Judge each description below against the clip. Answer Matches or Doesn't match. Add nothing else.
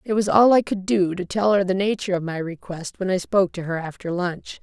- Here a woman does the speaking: Matches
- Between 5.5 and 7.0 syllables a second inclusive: Matches